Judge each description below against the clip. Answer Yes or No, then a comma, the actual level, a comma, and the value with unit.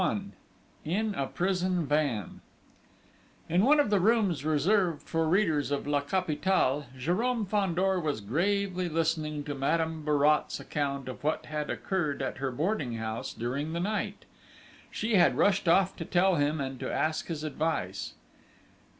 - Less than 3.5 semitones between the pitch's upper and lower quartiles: No, average, 4.7 semitones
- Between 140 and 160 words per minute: Yes, average, 150 wpm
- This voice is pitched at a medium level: Yes, medium, 160 Hz